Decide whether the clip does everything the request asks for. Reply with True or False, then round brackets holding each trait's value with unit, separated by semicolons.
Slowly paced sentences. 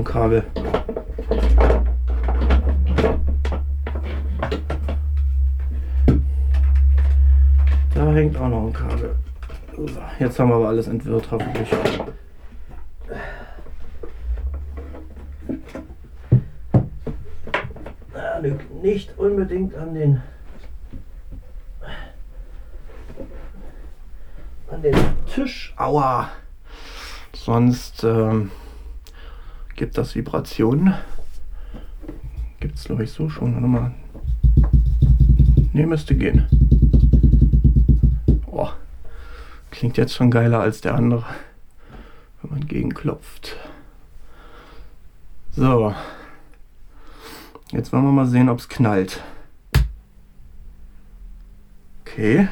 True (70 wpm)